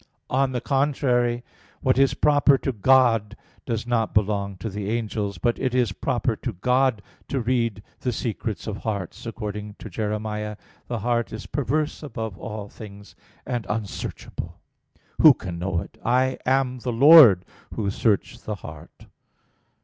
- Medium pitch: No, low, 115 Hz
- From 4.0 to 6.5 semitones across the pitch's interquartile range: No, average, 3.4 semitones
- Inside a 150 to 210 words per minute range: Yes, average, 155 wpm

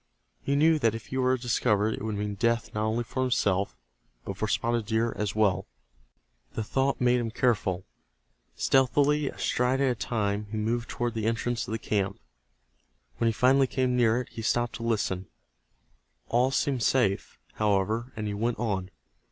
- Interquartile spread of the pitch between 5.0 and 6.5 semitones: No, average, 2.9 semitones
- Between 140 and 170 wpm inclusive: No, average, 180 wpm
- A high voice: No, low, 115 Hz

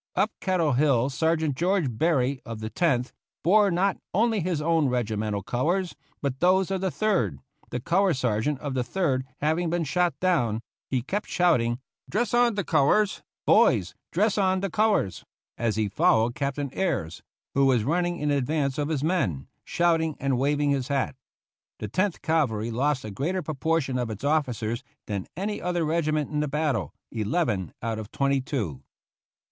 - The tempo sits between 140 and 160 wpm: No, average, 175 wpm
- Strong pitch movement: Yes, wide, 6.0 semitones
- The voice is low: No, medium, 145 Hz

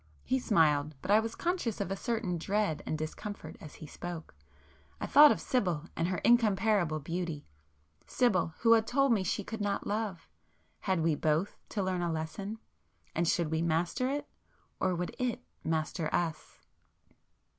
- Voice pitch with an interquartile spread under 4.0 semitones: No, wide, 5.4 semitones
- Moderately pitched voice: Yes, medium, 180 Hz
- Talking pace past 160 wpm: No, average, 155 wpm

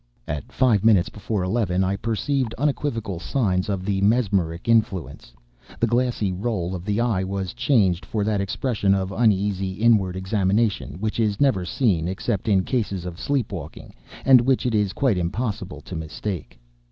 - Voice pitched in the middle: No, low, 100 Hz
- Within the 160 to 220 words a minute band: Yes, average, 165 wpm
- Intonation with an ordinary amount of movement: Yes, average, 3.8 semitones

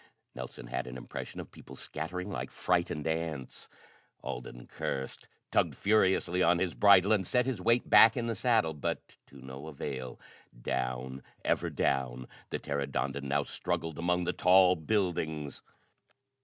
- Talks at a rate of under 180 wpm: Yes, average, 145 wpm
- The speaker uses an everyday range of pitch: No, wide, 5.7 semitones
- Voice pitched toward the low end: Yes, very low, 80 Hz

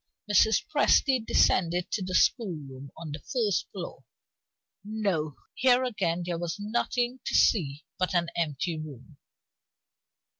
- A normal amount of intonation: No, wide, 6.0 semitones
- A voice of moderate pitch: Yes, medium, 180 Hz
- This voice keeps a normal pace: No, slow, 125 wpm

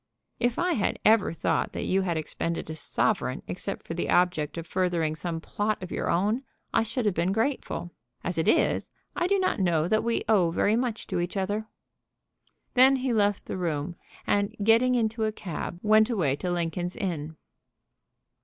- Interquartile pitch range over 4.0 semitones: Yes, average, 4.6 semitones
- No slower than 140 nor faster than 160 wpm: No, average, 185 wpm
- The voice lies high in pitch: Yes, high, 195 Hz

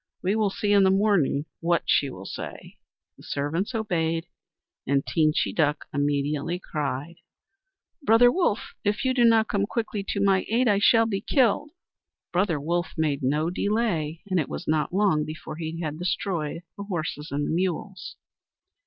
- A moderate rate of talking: Yes, average, 165 wpm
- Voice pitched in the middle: Yes, medium, 175 Hz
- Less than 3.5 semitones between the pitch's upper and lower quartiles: No, average, 5.1 semitones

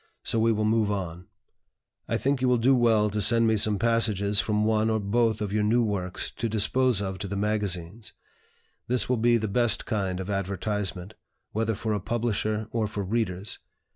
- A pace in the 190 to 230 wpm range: Yes, average, 195 wpm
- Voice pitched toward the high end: No, low, 105 Hz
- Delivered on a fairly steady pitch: Yes, narrow, 2.3 semitones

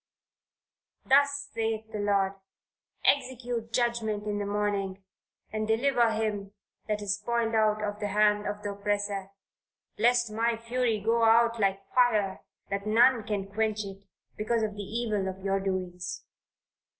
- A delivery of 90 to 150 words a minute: Yes, average, 145 wpm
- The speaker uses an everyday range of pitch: No, narrow, 2.3 semitones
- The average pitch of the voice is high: Yes, high, 215 Hz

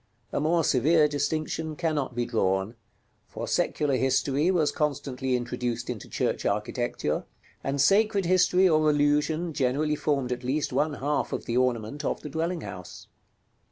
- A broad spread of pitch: No, average, 3.9 semitones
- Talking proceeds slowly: No, average, 150 wpm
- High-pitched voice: No, medium, 145 Hz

